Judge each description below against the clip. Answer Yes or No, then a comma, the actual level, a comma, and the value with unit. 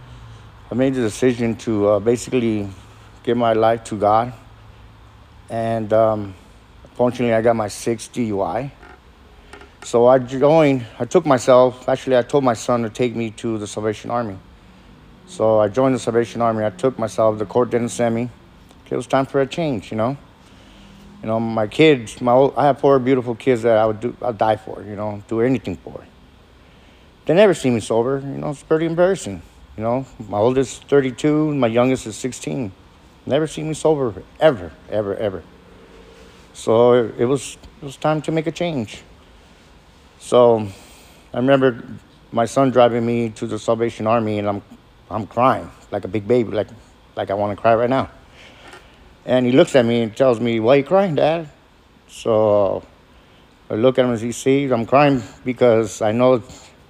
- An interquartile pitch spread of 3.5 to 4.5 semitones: Yes, average, 3.8 semitones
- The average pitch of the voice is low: Yes, low, 115 Hz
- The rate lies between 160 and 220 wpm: Yes, average, 180 wpm